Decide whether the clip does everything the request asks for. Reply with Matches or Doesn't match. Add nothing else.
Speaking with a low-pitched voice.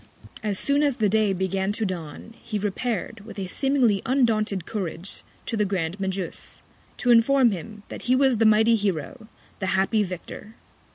Doesn't match